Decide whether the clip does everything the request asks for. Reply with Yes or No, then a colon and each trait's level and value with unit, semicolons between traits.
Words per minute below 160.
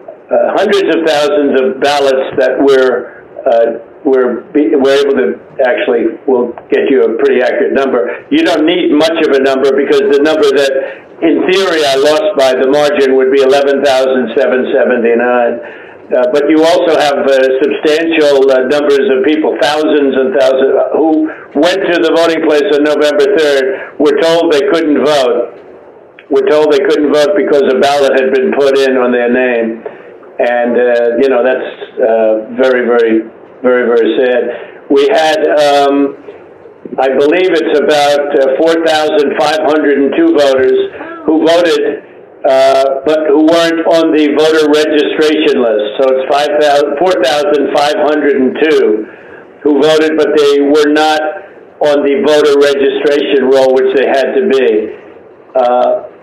Yes: average, 150 wpm